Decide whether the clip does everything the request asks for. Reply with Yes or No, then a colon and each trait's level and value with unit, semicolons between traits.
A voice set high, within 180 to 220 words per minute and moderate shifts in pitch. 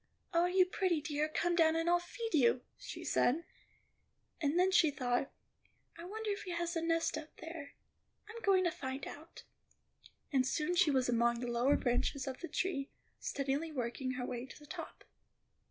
Yes: very high, 310 Hz; average, 185 wpm; average, 4.8 semitones